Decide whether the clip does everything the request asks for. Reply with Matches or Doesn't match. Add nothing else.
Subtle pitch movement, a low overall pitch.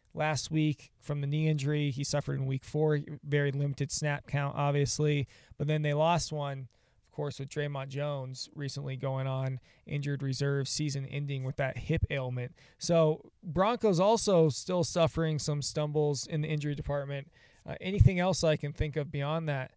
Doesn't match